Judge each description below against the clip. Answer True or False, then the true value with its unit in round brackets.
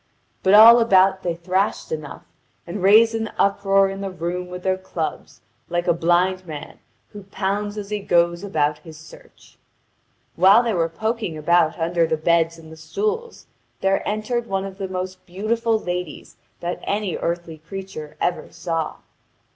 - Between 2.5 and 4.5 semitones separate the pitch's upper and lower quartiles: True (3.1 semitones)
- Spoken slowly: False (165 wpm)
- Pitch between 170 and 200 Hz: True (185 Hz)